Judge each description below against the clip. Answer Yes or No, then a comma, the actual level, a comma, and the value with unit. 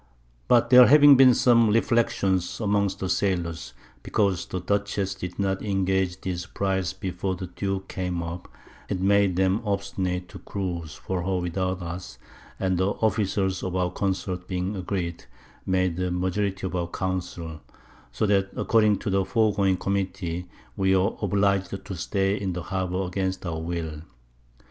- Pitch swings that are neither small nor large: No, narrow, 1.8 semitones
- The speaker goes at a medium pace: Yes, average, 155 wpm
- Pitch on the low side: Yes, very low, 95 Hz